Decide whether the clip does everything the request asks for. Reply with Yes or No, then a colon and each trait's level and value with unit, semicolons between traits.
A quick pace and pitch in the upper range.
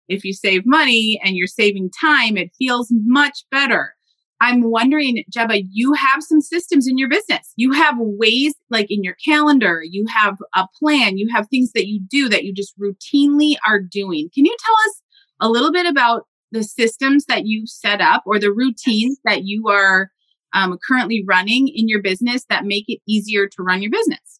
No: average, 195 wpm; high, 230 Hz